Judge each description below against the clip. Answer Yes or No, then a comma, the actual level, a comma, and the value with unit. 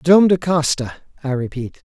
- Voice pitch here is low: No, medium, 145 Hz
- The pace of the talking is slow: Yes, slow, 125 wpm